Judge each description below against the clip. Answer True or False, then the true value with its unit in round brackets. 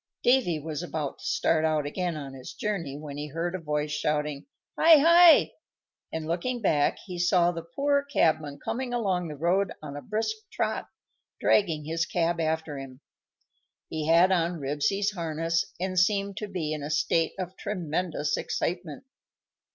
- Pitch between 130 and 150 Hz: False (165 Hz)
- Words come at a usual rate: True (165 wpm)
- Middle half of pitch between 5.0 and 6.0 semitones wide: False (4.0 semitones)